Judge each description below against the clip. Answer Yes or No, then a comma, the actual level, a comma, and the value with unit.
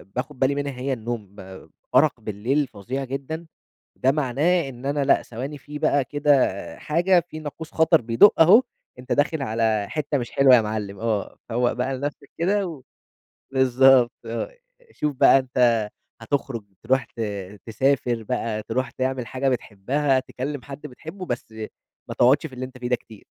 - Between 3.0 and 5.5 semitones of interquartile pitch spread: Yes, average, 3.3 semitones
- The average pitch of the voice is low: Yes, low, 130 Hz